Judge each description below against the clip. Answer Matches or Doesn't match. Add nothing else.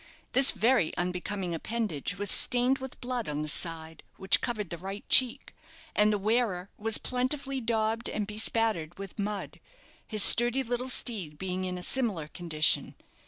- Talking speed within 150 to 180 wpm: Matches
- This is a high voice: Matches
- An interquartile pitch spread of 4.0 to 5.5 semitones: Matches